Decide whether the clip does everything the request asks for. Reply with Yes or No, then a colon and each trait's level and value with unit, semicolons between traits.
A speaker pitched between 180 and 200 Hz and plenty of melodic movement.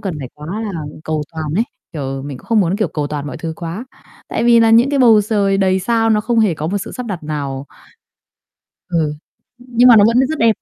Yes: high, 195 Hz; wide, 6.8 semitones